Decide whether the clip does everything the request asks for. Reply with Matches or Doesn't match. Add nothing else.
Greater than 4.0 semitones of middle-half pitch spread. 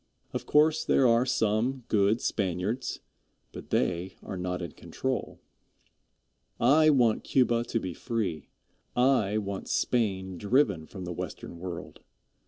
Matches